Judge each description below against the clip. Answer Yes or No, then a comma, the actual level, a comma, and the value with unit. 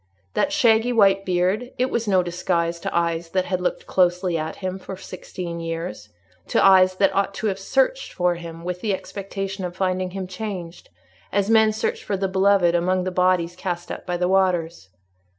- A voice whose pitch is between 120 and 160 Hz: No, medium, 185 Hz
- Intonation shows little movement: Yes, narrow, 2.1 semitones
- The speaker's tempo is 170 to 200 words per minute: Yes, average, 185 wpm